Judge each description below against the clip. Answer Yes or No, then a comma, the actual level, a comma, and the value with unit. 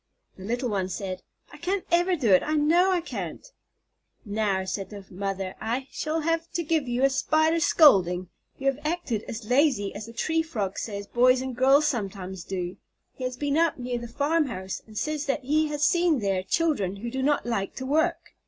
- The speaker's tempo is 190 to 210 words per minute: Yes, fast, 205 wpm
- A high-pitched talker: Yes, very high, 255 Hz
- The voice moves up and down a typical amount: No, wide, 7.4 semitones